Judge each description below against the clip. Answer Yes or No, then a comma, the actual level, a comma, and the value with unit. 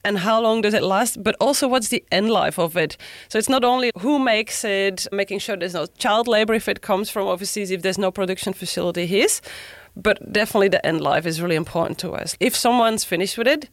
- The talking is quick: Yes, fast, 230 wpm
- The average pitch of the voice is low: No, high, 205 Hz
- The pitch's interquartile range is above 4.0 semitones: No, average, 3.2 semitones